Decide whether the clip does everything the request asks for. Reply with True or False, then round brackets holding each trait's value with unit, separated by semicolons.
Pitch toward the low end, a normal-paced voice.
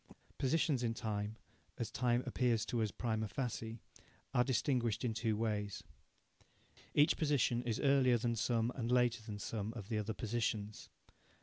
True (115 Hz; 150 wpm)